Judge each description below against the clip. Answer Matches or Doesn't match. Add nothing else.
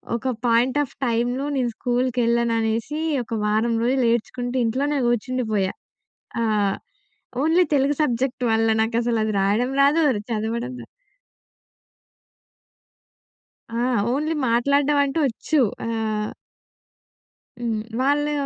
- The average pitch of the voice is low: Doesn't match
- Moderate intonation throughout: Matches